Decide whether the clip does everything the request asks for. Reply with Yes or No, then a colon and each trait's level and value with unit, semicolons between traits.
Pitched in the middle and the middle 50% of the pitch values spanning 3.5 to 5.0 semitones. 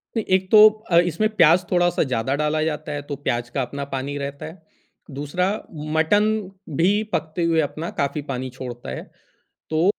Yes: medium, 155 Hz; average, 4.0 semitones